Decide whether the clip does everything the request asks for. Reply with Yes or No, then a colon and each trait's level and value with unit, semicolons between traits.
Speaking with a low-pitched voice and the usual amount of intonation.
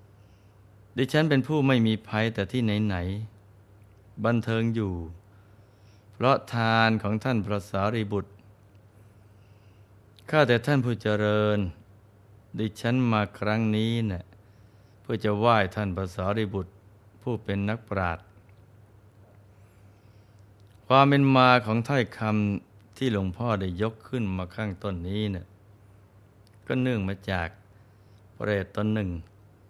No: low, 105 Hz; narrow, 1.5 semitones